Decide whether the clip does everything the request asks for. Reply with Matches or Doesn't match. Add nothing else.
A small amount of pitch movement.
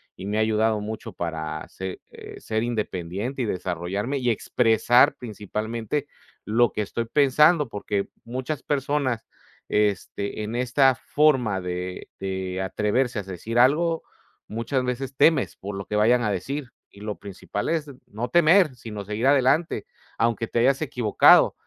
Doesn't match